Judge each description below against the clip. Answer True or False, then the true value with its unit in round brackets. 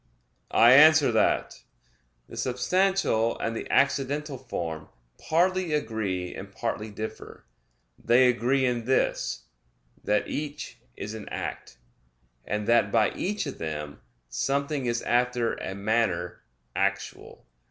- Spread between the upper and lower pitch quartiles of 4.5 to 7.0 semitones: True (5.1 semitones)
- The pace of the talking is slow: True (120 wpm)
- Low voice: True (120 Hz)